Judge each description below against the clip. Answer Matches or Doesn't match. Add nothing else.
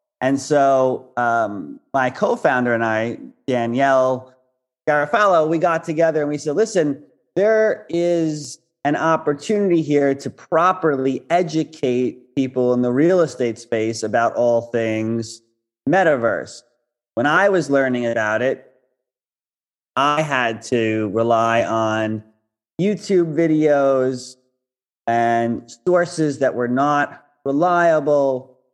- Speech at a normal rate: Doesn't match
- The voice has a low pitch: Matches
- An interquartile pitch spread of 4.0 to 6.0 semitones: Matches